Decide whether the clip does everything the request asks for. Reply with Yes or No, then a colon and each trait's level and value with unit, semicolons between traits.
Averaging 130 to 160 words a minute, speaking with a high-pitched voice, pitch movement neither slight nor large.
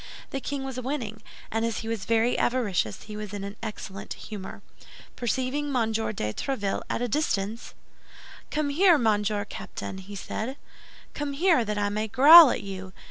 No: average, 170 wpm; high, 225 Hz; average, 4.6 semitones